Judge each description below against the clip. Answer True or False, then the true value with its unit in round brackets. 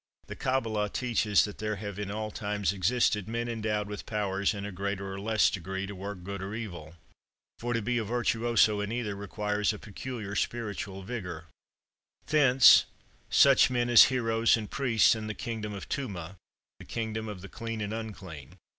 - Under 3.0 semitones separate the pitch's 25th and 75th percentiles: True (2.6 semitones)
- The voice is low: True (105 Hz)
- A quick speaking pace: False (180 wpm)